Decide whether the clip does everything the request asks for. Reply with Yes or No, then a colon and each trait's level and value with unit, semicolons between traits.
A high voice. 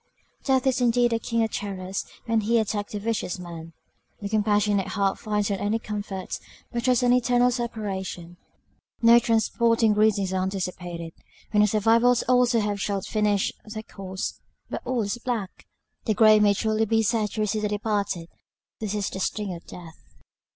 Yes: high, 210 Hz